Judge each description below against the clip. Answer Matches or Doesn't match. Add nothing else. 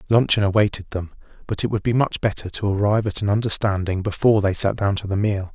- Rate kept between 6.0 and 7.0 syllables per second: Matches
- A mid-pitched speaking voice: Doesn't match